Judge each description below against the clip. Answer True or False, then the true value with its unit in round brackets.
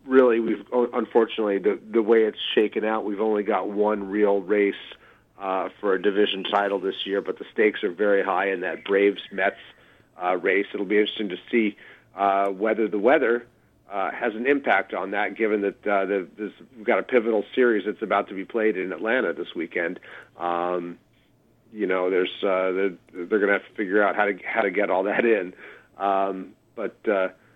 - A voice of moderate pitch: False (100 Hz)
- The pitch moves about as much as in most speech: False (1.9 semitones)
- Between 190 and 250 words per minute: True (200 wpm)